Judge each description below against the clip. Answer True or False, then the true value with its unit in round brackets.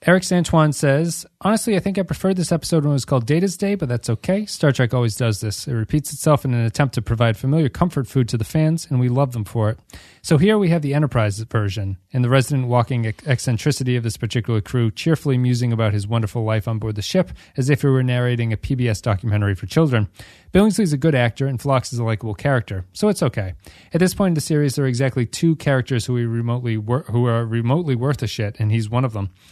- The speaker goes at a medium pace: False (235 wpm)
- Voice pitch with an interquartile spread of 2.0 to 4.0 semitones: False (4.9 semitones)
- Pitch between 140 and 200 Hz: False (125 Hz)